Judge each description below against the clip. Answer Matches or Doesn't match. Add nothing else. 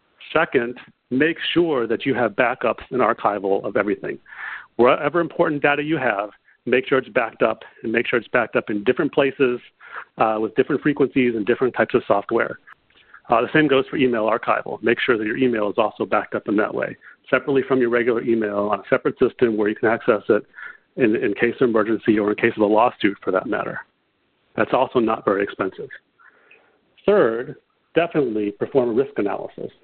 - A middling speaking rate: Matches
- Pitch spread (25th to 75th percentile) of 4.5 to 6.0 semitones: Matches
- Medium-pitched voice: Doesn't match